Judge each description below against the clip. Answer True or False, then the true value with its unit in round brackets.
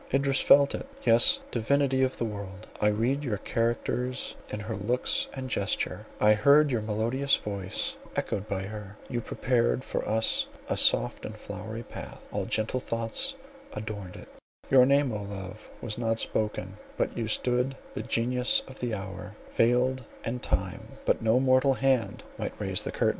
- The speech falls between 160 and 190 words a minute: True (165 wpm)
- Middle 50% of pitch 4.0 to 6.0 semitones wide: False (3.5 semitones)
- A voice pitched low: True (115 Hz)